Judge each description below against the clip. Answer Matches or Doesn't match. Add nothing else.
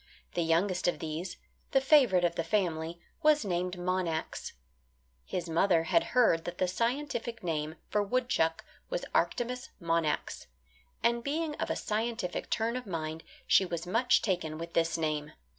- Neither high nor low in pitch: Matches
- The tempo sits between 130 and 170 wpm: Matches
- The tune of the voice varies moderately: Doesn't match